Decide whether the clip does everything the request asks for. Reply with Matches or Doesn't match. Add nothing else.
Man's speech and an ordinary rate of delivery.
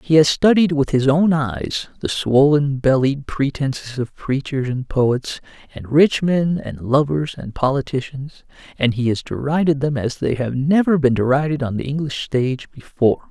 Matches